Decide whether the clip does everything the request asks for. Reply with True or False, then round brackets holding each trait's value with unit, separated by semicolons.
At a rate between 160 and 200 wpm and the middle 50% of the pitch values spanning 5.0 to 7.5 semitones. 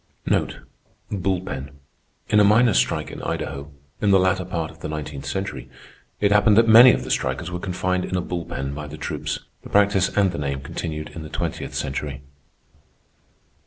True (180 wpm; 5.3 semitones)